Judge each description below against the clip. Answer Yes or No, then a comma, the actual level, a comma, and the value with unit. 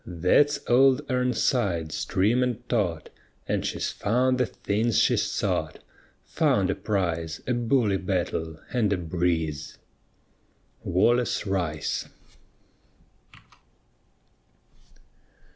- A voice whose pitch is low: Yes, low, 100 Hz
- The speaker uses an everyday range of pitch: No, wide, 6.3 semitones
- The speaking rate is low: Yes, slow, 95 wpm